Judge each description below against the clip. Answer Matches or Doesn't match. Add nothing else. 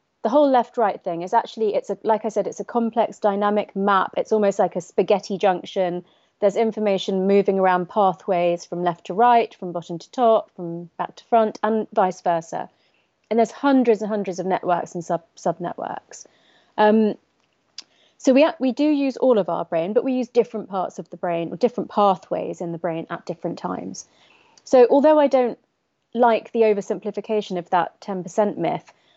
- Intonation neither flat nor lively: Matches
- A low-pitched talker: Doesn't match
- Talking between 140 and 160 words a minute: Doesn't match